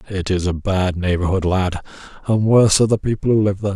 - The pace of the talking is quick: Yes, fast, 225 wpm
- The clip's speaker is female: No, male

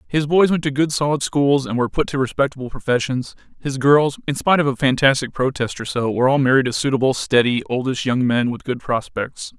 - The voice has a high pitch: No, low, 135 Hz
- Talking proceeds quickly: Yes, fast, 220 wpm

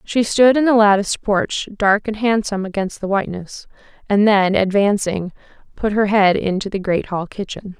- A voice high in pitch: Yes, high, 205 Hz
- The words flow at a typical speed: Yes, average, 175 wpm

